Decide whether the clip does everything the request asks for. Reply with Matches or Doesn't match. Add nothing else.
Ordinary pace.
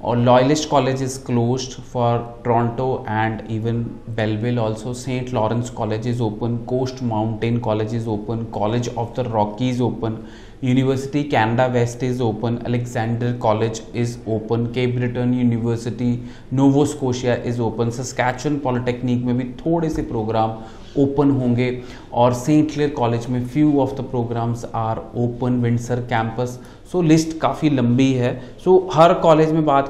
Matches